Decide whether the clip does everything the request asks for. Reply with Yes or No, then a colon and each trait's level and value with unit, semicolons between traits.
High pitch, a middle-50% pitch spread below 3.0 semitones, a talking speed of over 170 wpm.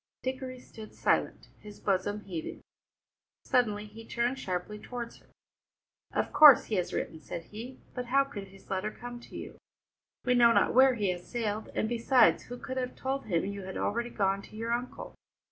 No: high, 225 Hz; average, 3.6 semitones; average, 185 wpm